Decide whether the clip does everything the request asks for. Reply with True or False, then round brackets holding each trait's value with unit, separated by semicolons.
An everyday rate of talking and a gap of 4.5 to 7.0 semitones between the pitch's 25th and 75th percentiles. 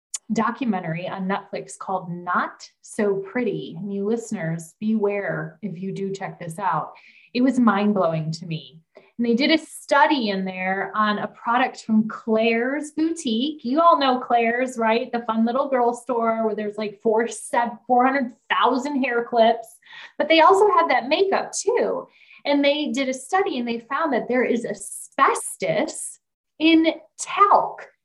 True (160 wpm; 5.2 semitones)